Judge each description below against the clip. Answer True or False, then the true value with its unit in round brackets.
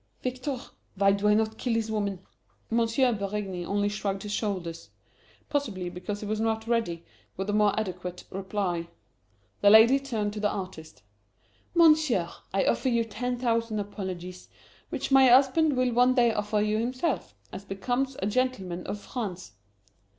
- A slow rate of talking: False (160 wpm)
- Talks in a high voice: True (210 Hz)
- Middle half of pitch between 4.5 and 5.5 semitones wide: False (4.0 semitones)